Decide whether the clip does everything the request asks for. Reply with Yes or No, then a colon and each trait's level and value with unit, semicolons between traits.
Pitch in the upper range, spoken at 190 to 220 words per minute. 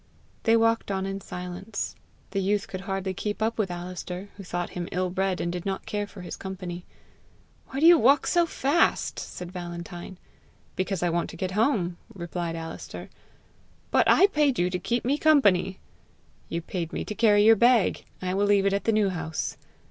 Yes: high, 195 Hz; average, 195 wpm